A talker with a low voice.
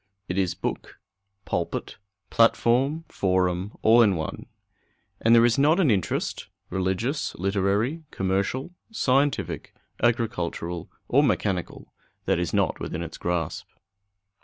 Yes: low, 105 Hz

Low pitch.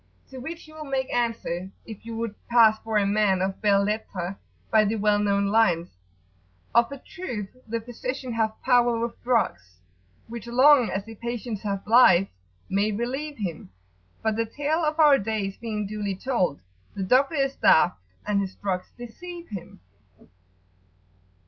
No: high, 225 Hz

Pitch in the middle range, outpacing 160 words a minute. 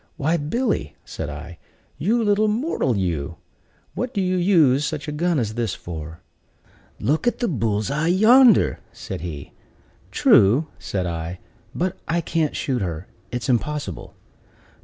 No: medium, 145 Hz; average, 150 wpm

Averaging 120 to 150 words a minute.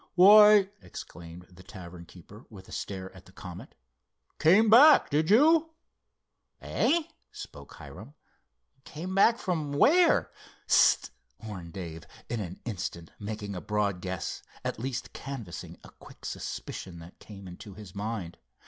Yes: average, 140 wpm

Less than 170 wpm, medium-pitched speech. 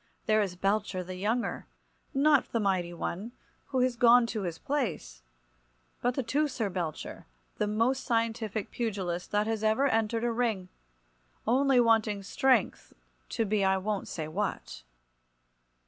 No: average, 140 wpm; high, 215 Hz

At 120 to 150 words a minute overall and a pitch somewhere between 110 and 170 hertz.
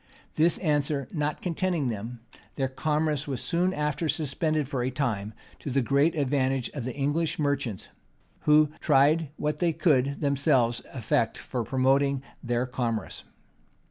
Yes: average, 140 wpm; medium, 140 Hz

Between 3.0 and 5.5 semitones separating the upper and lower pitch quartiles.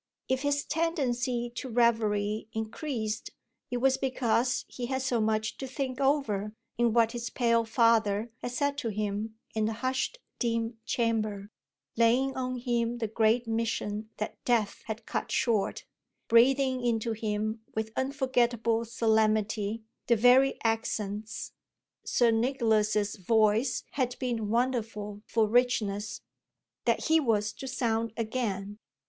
No: narrow, 2.5 semitones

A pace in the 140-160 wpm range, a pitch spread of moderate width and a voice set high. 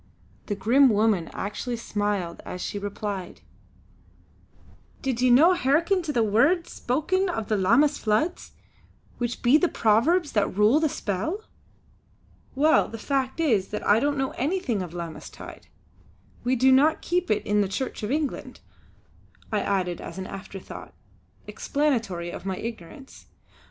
No: average, 150 wpm; wide, 6.3 semitones; high, 235 Hz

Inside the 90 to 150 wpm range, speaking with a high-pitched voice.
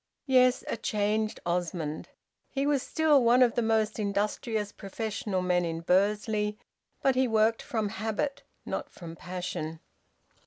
Yes: average, 140 wpm; high, 215 Hz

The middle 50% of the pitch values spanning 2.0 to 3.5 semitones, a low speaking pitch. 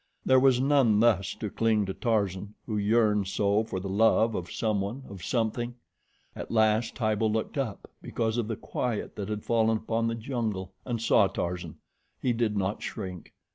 Yes: narrow, 2.4 semitones; low, 110 Hz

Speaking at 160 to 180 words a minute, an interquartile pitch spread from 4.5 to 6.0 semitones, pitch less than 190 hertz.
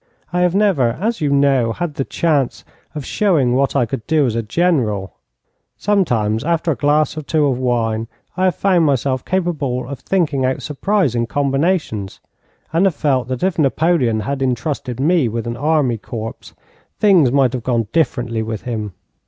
Yes: average, 175 wpm; wide, 5.5 semitones; medium, 140 Hz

